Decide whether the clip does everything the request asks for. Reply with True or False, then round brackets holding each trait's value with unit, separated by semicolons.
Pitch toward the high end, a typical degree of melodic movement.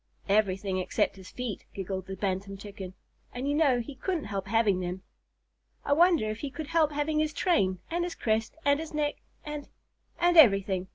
False (225 Hz; 7.6 semitones)